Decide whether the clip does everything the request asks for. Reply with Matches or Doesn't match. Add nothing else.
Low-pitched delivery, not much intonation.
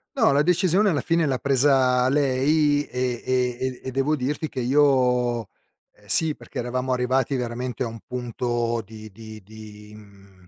Doesn't match